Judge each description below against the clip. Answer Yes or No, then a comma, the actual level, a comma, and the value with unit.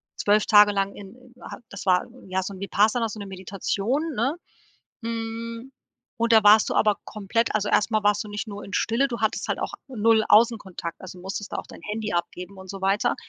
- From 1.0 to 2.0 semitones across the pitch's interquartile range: No, narrow, 2.5 semitones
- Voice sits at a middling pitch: No, high, 210 Hz